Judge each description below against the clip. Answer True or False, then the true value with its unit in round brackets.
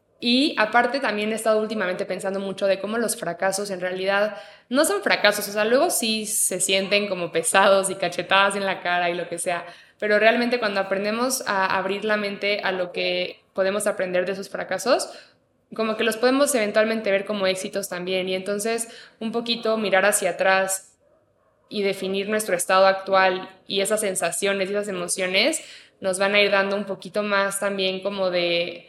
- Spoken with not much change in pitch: True (2.2 semitones)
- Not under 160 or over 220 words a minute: True (185 wpm)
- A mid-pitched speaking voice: False (195 Hz)